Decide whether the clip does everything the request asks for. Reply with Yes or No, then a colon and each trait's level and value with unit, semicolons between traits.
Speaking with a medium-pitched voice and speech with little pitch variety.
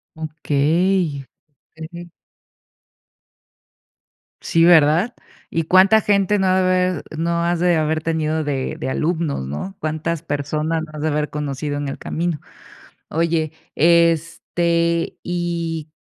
Yes: medium, 165 Hz; narrow, 2.2 semitones